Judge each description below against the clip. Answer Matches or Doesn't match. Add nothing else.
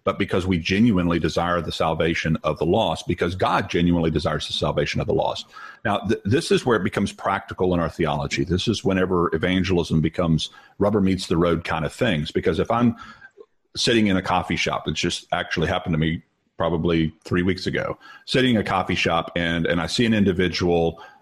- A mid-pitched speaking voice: Doesn't match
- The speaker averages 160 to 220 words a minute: Matches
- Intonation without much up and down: Matches